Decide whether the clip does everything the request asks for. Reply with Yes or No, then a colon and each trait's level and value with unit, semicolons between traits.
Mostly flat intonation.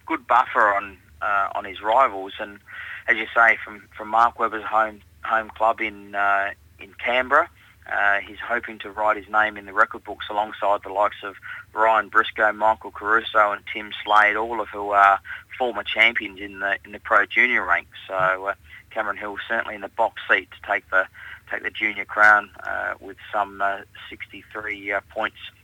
Yes: narrow, 1.7 semitones